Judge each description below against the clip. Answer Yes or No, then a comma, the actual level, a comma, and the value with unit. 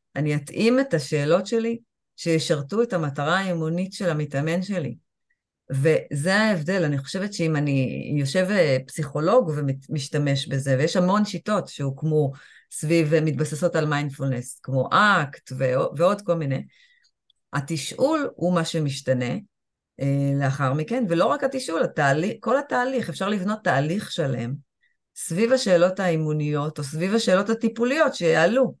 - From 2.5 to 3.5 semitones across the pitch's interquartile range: No, average, 5.2 semitones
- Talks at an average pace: Yes, average, 120 wpm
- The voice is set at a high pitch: No, medium, 165 Hz